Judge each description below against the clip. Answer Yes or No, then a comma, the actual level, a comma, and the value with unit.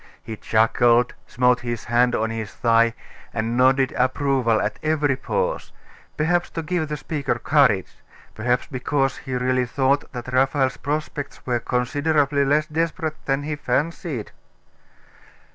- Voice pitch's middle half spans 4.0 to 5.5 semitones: No, average, 3.5 semitones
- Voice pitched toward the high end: No, low, 130 Hz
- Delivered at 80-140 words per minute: Yes, slow, 135 wpm